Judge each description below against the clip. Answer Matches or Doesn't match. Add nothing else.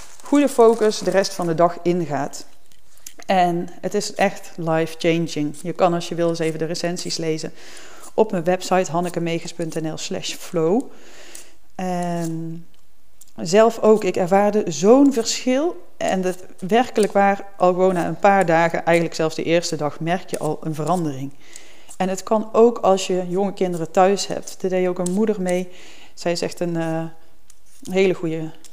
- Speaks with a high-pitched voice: Doesn't match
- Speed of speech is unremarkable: Matches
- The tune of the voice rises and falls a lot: Doesn't match